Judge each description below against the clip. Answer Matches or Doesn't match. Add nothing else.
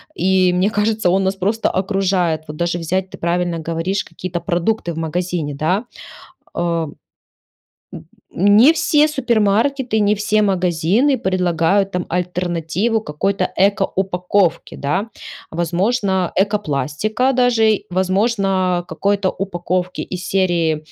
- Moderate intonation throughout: Matches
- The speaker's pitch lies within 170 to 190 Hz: Matches